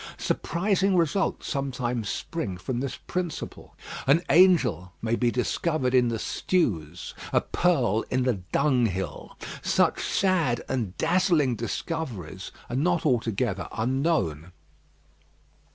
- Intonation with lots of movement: Yes, wide, 7.0 semitones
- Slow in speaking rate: Yes, slow, 110 wpm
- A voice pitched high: No, low, 125 Hz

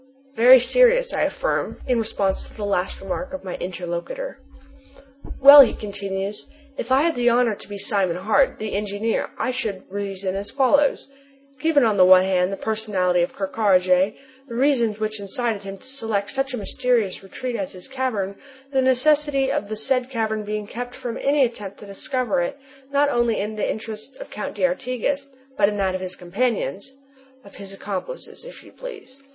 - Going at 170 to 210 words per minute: Yes, average, 190 wpm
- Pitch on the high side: Yes, high, 220 Hz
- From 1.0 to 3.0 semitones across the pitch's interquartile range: No, average, 5.0 semitones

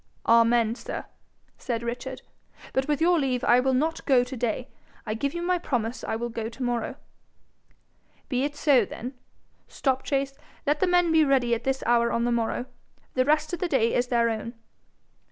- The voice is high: Yes, very high, 255 Hz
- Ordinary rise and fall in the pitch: Yes, average, 3.4 semitones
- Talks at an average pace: Yes, average, 190 wpm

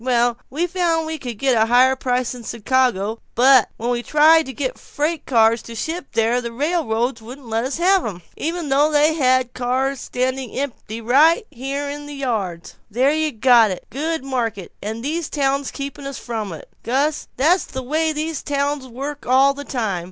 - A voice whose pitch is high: Yes, very high, 265 Hz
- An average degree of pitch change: Yes, average, 3.8 semitones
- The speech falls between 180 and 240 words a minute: Yes, average, 190 wpm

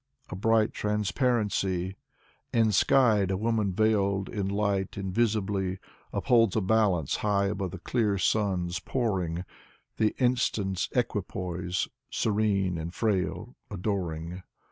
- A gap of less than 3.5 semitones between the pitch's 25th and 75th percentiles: Yes, average, 2.8 semitones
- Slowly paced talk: Yes, slow, 105 wpm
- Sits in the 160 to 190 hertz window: No, low, 100 Hz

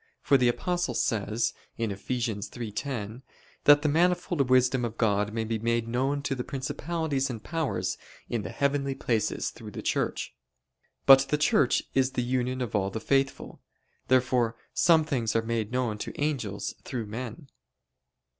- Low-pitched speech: Yes, low, 125 Hz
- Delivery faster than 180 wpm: No, average, 155 wpm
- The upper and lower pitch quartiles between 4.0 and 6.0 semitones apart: No, average, 3.5 semitones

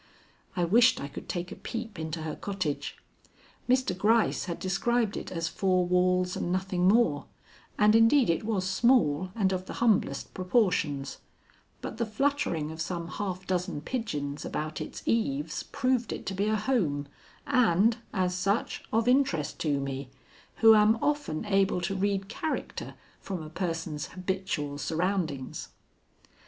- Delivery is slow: No, average, 150 wpm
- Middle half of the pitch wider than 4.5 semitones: Yes, average, 5.0 semitones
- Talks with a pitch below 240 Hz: Yes, medium, 185 Hz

